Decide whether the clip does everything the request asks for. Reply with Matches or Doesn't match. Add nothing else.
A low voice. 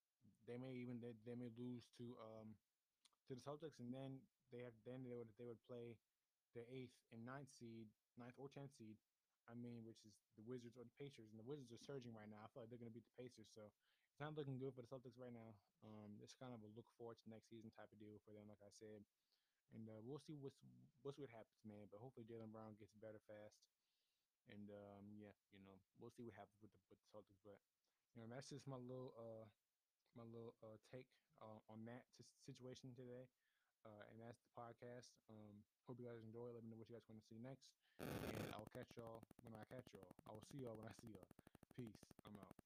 Matches